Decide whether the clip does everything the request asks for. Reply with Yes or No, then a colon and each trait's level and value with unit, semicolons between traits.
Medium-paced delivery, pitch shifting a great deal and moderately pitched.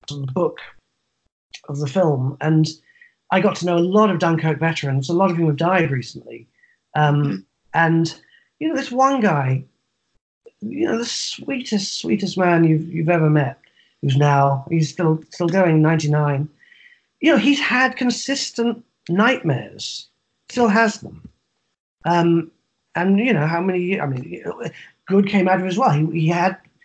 Yes: average, 160 wpm; wide, 6.5 semitones; medium, 175 Hz